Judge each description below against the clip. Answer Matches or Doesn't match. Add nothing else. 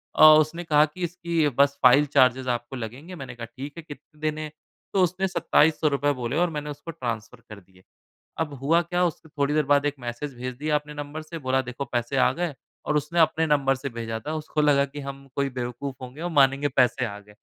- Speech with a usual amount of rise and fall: Matches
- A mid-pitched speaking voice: Matches